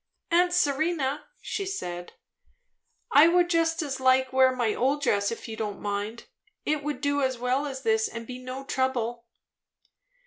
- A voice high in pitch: Yes, very high, 260 Hz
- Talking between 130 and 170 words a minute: Yes, average, 165 wpm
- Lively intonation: No, average, 4.1 semitones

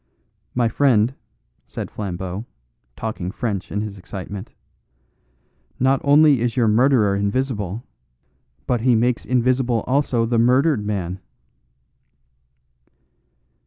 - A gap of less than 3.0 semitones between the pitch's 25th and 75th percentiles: No, average, 3.9 semitones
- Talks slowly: Yes, slow, 100 wpm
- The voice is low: Yes, low, 115 Hz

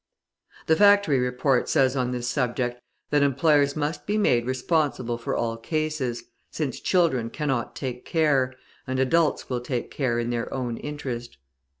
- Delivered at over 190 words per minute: No, average, 155 wpm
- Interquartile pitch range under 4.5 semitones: Yes, average, 3.6 semitones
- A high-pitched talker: No, low, 130 Hz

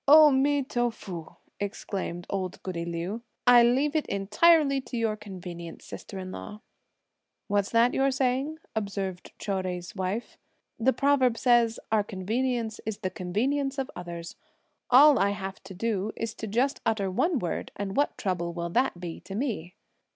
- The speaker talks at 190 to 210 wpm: No, average, 165 wpm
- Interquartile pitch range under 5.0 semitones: No, wide, 5.5 semitones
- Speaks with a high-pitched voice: Yes, high, 215 Hz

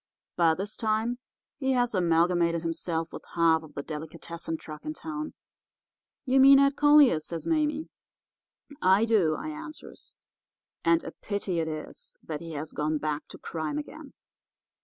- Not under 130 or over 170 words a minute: Yes, average, 150 wpm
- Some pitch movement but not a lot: No, wide, 8.8 semitones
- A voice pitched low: No, medium, 170 Hz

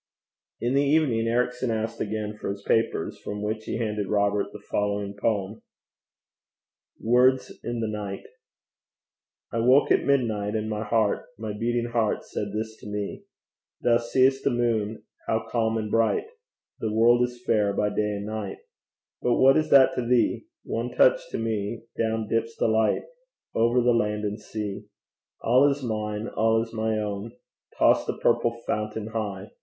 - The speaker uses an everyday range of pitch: No, narrow, 2.2 semitones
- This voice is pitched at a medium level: No, low, 110 Hz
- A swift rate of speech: No, average, 165 wpm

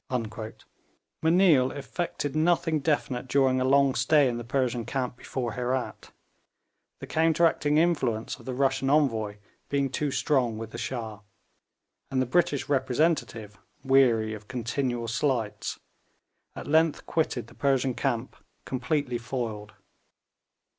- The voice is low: Yes, low, 130 Hz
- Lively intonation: No, average, 3.5 semitones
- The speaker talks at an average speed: No, slow, 125 wpm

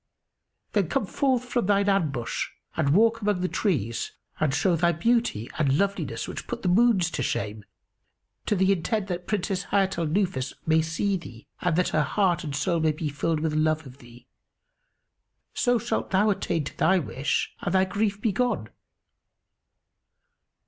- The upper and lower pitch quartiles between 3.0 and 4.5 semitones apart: No, average, 4.9 semitones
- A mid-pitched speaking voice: Yes, medium, 180 Hz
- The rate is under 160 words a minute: No, average, 170 wpm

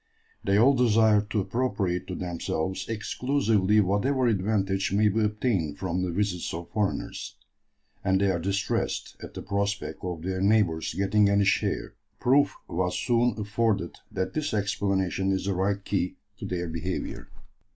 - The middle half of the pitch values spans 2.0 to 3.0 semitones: Yes, narrow, 2.6 semitones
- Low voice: Yes, low, 100 Hz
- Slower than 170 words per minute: Yes, average, 150 wpm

